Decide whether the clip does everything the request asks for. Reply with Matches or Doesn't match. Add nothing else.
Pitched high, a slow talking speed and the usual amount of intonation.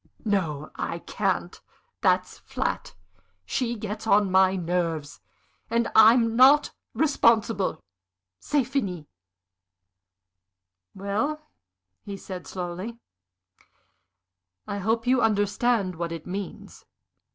Matches